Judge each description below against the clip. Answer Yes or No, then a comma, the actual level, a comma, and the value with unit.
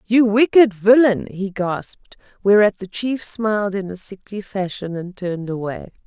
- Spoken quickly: No, average, 160 wpm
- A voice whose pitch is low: No, high, 200 Hz